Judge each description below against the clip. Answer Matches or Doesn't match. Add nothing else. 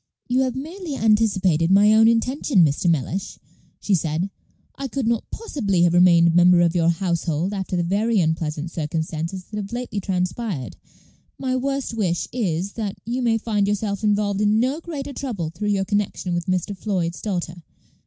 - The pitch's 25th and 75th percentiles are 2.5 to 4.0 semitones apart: Doesn't match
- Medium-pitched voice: Doesn't match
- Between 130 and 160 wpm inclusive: Doesn't match